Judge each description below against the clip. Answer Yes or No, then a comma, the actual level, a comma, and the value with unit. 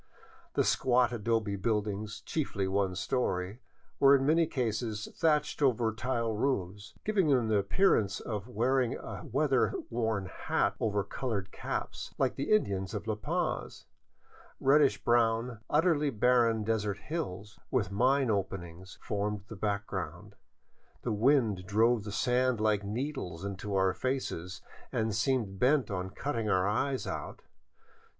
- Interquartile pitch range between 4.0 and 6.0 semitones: Yes, average, 4.3 semitones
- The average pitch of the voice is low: Yes, low, 110 Hz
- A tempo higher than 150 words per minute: No, slow, 135 wpm